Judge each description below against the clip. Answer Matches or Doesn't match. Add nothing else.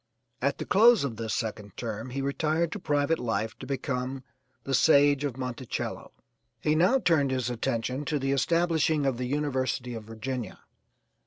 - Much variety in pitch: Doesn't match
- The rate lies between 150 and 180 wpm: Matches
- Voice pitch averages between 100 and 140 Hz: Matches